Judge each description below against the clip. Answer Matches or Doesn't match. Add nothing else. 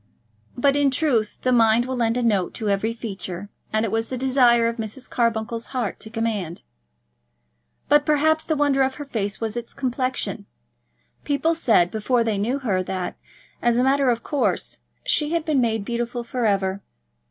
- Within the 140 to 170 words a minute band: Doesn't match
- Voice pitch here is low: Doesn't match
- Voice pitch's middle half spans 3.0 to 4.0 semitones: Matches